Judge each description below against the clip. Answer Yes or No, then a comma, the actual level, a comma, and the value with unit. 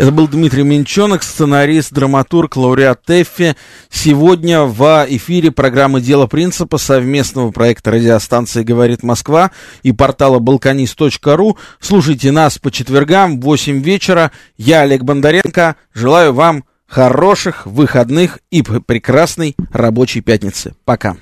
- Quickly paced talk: No, average, 115 wpm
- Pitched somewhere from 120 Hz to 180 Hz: Yes, medium, 140 Hz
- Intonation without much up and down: No, average, 4.0 semitones